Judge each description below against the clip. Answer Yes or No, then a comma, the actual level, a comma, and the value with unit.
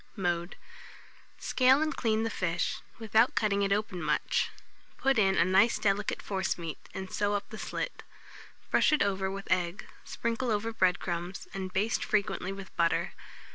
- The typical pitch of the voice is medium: No, high, 200 Hz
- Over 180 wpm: No, average, 160 wpm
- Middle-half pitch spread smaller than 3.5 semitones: Yes, average, 3.0 semitones